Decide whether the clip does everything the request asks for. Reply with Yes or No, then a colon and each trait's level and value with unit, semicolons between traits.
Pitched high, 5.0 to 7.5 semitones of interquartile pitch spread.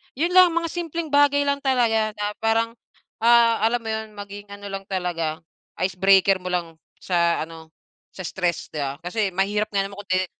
No: high, 205 Hz; average, 4.2 semitones